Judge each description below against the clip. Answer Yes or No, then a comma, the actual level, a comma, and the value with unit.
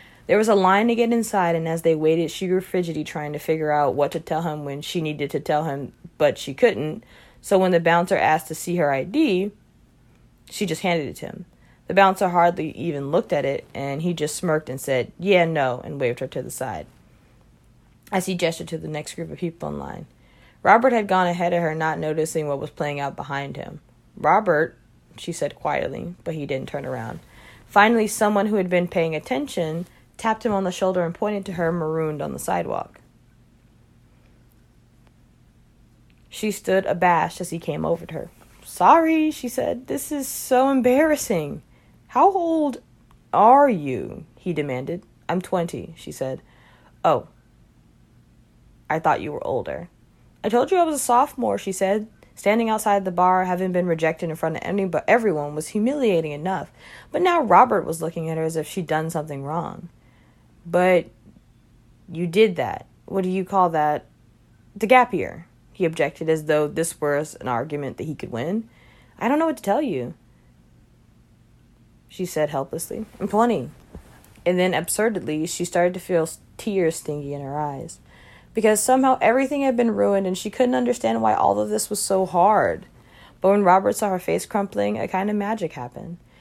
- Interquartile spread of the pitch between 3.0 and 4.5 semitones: No, average, 5.2 semitones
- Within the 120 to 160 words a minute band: No, average, 185 wpm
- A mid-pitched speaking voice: Yes, medium, 175 Hz